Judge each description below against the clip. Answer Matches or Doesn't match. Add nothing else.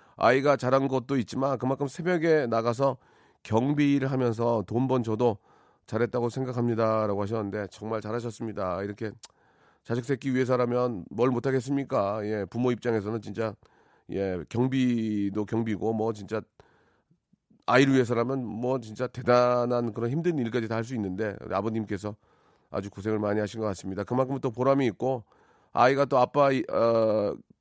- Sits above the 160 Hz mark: Doesn't match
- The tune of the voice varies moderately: Matches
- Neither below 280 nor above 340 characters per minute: Matches